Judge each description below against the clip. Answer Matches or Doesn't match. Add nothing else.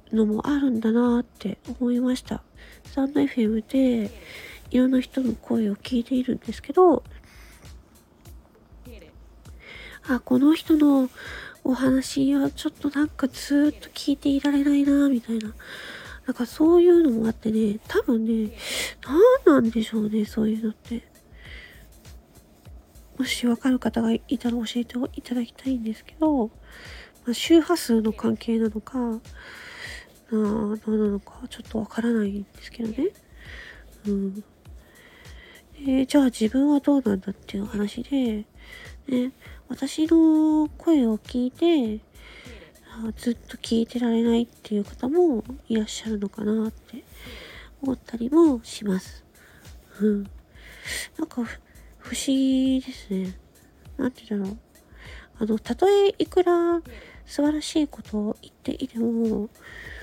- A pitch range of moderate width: Matches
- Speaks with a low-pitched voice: Doesn't match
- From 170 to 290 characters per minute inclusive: Matches